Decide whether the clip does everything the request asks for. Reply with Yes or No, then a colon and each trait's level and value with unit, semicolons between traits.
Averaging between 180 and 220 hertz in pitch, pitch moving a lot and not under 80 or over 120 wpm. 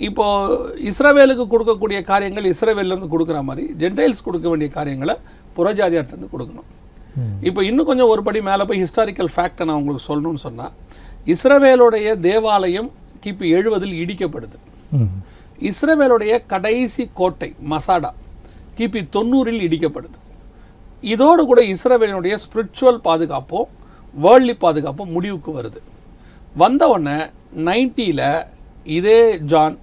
Yes: medium, 185 Hz; wide, 6.9 semitones; average, 105 wpm